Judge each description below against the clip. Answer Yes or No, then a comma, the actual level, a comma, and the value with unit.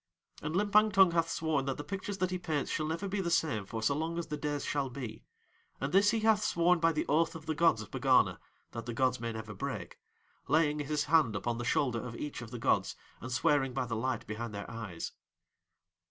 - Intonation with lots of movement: Yes, wide, 5.8 semitones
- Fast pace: Yes, fast, 230 wpm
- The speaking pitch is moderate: Yes, medium, 145 Hz